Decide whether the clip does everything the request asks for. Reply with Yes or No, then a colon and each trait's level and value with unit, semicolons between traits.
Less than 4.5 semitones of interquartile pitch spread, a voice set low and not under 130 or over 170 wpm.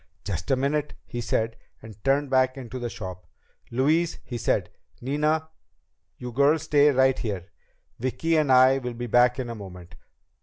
Yes: average, 3.8 semitones; low, 130 Hz; average, 165 wpm